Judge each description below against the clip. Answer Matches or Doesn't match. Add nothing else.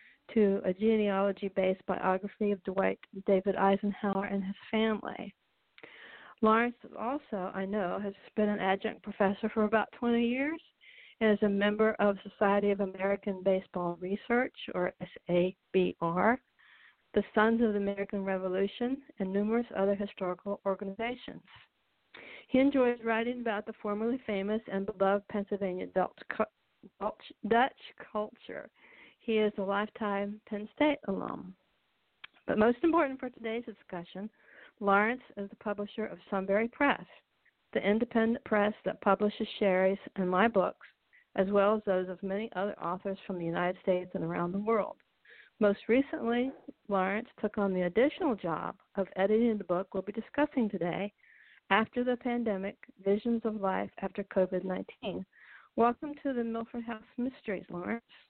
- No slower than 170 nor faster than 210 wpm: Doesn't match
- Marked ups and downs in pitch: Doesn't match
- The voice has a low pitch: Doesn't match